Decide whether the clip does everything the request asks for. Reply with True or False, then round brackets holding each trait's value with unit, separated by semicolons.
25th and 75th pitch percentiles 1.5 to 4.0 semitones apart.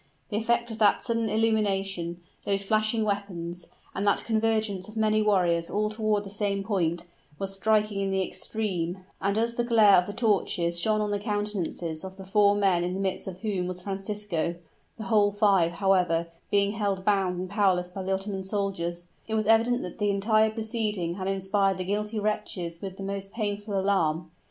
True (2.4 semitones)